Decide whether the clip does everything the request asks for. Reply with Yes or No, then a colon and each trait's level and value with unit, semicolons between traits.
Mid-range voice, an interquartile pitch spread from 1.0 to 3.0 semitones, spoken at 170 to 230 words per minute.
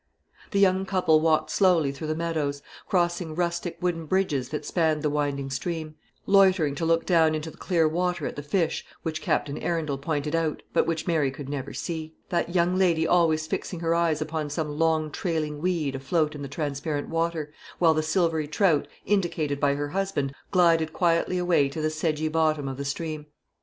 Yes: medium, 160 Hz; narrow, 2.5 semitones; average, 190 wpm